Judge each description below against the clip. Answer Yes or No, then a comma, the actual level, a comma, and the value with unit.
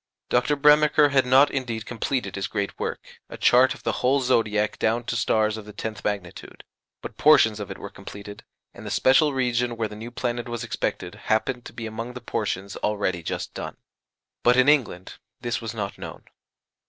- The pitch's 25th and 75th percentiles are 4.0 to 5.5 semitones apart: No, average, 3.3 semitones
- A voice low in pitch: Yes, low, 115 Hz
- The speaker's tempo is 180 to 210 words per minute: Yes, average, 190 wpm